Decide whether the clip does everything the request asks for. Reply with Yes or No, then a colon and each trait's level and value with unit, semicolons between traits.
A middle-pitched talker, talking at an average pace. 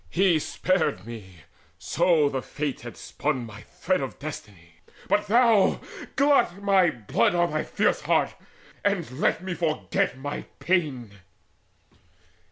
No: medium, 155 Hz; slow, 130 wpm